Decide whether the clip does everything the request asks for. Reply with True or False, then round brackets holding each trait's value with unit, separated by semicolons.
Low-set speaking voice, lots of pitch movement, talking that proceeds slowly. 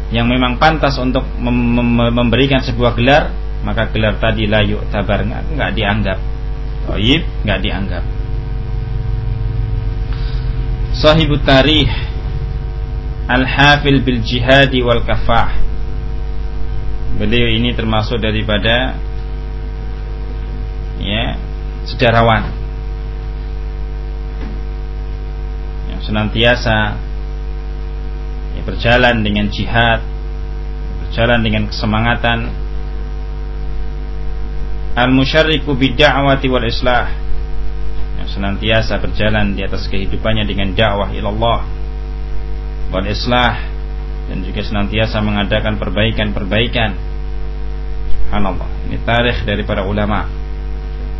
True (110 Hz; 5.7 semitones; 75 wpm)